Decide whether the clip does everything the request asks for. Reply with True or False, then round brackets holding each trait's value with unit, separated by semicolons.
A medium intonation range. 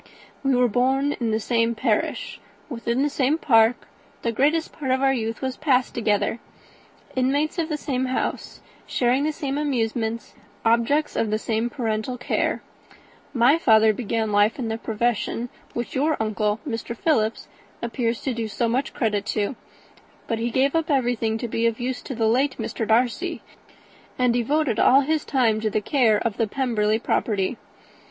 True (3.1 semitones)